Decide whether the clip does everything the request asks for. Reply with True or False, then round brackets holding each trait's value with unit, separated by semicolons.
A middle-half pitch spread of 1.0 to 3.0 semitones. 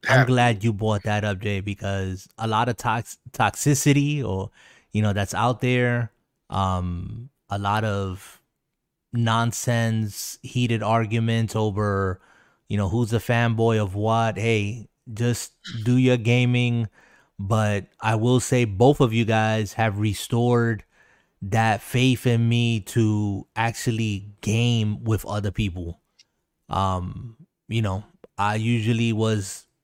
True (2.6 semitones)